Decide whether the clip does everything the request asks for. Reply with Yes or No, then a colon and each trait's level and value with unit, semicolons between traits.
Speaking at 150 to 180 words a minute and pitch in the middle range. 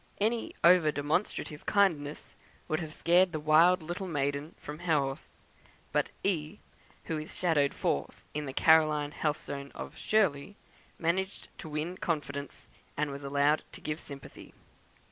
No: average, 140 wpm; medium, 155 Hz